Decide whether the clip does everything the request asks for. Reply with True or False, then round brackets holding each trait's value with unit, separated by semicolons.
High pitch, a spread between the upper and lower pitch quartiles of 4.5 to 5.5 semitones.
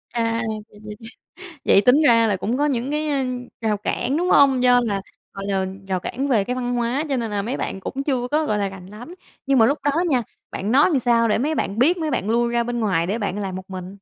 True (235 Hz; 4.8 semitones)